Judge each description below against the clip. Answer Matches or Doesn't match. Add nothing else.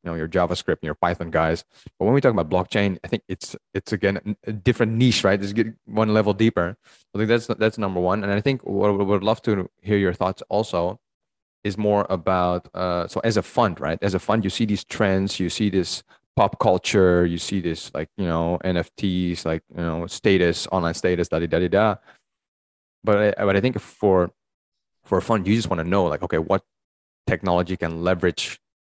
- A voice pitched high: Doesn't match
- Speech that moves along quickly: Matches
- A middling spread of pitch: Matches